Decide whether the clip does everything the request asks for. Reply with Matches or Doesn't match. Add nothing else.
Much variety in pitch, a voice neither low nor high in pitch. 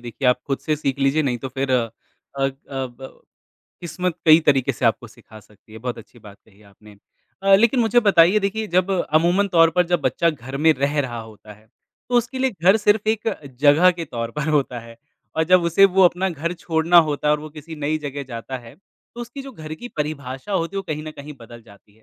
Matches